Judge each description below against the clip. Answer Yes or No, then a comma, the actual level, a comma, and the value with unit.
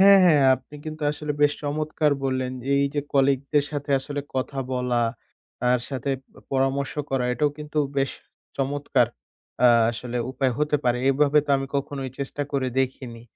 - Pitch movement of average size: No, narrow, 2.1 semitones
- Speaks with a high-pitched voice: No, medium, 140 Hz